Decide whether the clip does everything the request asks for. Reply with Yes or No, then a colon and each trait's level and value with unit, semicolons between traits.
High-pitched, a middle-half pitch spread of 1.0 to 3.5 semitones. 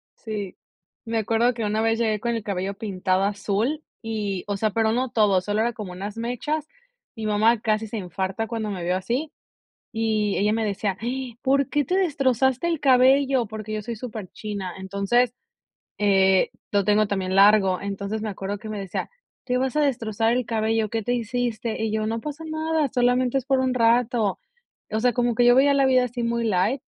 Yes: high, 225 Hz; average, 3.2 semitones